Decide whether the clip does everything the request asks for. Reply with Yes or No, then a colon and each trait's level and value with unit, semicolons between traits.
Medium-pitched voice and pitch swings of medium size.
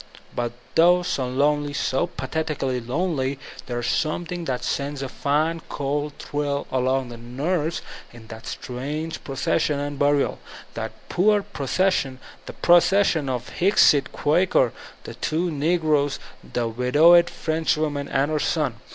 Yes: medium, 145 Hz; average, 3.7 semitones